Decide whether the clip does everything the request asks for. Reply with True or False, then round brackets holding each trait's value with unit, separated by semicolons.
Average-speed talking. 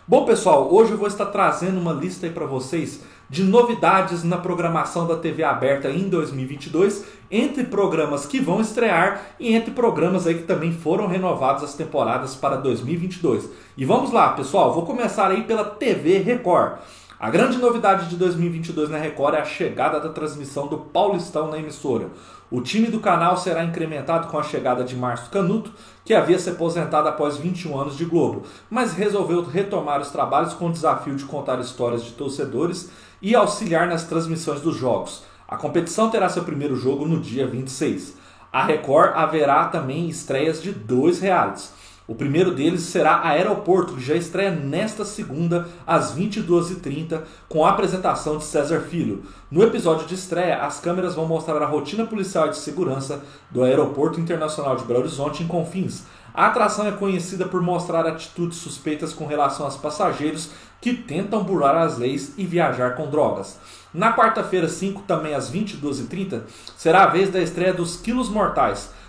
True (170 wpm)